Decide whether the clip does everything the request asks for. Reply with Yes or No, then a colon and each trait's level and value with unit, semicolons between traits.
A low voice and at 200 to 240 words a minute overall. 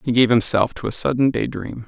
No: low, 120 Hz; fast, 255 wpm